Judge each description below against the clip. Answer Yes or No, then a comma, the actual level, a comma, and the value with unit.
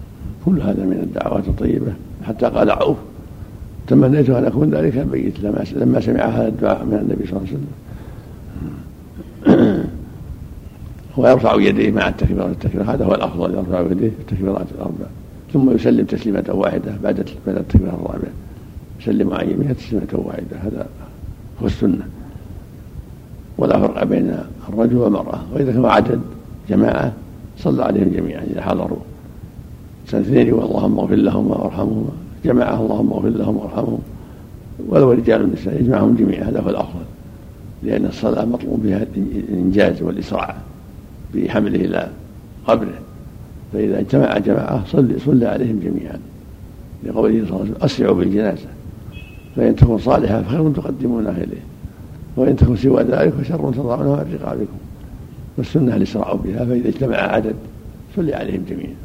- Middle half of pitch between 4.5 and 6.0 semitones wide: No, average, 3.7 semitones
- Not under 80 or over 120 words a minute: No, average, 130 wpm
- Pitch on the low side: Yes, low, 105 Hz